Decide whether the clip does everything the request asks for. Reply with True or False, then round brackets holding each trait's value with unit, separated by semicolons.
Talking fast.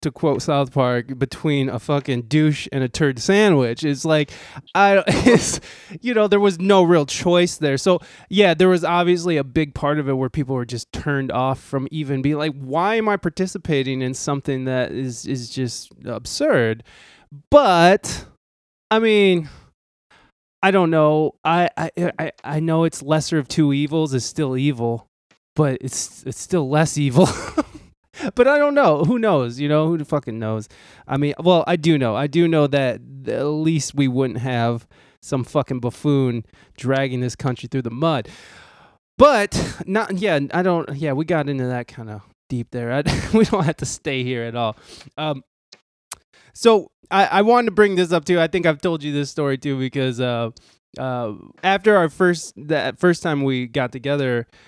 False (185 wpm)